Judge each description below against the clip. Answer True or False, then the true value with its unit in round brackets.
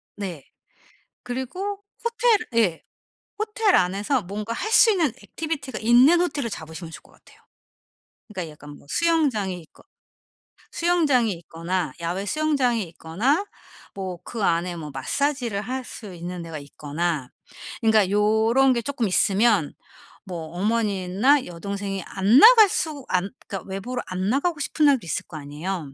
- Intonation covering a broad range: True (7.6 semitones)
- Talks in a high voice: True (210 Hz)